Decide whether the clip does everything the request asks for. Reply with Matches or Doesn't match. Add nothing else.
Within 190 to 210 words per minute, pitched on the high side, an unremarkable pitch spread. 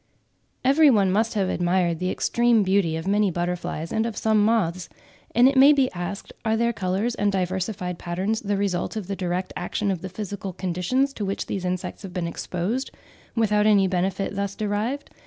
Matches